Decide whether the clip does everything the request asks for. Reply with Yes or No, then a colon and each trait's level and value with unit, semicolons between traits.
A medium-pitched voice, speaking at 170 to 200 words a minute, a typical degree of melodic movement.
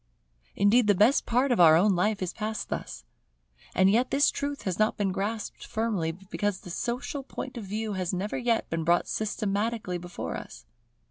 No: high, 210 Hz; average, 185 wpm; average, 3.8 semitones